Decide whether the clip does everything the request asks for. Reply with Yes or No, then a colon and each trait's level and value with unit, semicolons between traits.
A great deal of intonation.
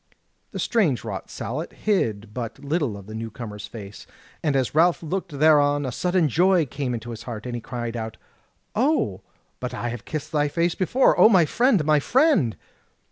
Yes: wide, 6.9 semitones